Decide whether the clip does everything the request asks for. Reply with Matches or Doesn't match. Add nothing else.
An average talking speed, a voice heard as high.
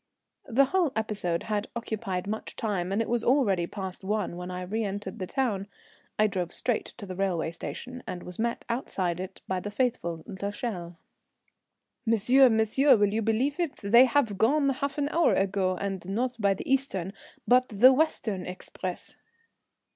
Matches